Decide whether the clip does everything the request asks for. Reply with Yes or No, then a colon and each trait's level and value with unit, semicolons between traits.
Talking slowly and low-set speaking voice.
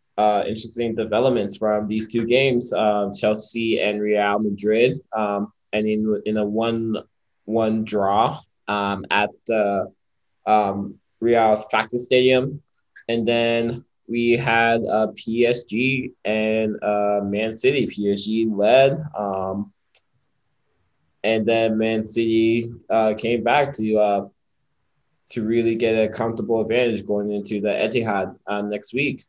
Yes: slow, 130 wpm; low, 110 Hz